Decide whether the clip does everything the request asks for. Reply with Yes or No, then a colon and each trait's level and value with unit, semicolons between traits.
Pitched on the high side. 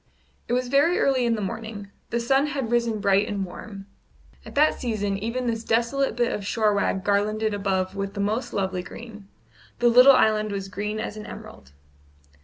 Yes: high, 215 Hz